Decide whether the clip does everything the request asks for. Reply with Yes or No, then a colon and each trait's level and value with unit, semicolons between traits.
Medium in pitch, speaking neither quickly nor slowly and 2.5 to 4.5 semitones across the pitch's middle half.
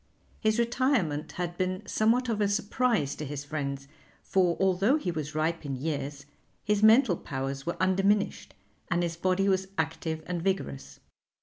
No: medium, 180 Hz; average, 155 wpm; average, 5.3 semitones